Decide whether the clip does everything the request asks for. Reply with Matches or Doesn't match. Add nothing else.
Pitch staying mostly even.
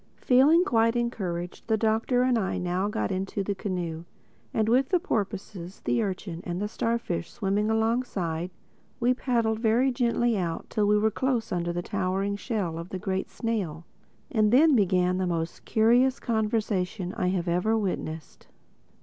Doesn't match